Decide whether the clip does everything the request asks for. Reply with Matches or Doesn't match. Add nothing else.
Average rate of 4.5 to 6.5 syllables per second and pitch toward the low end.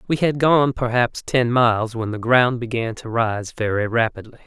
Matches